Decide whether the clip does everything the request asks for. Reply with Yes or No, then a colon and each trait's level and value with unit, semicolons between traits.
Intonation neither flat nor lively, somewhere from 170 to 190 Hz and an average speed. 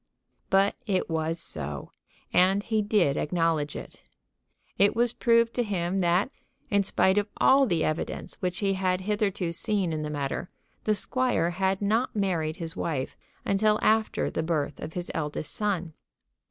Yes: average, 4.2 semitones; medium, 185 Hz; average, 160 wpm